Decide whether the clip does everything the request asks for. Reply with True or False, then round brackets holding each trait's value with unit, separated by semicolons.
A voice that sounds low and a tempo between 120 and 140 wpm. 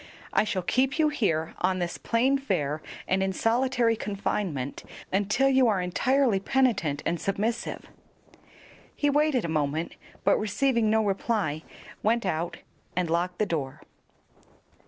False (205 Hz; 135 wpm)